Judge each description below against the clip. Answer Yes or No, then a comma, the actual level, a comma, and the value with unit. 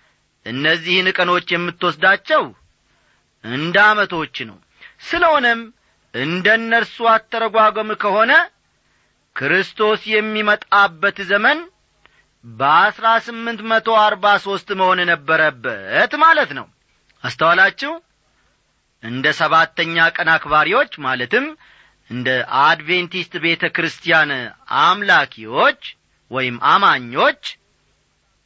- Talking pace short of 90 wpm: Yes, average, 75 wpm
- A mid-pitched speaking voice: No, high, 195 Hz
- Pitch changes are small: No, wide, 5.4 semitones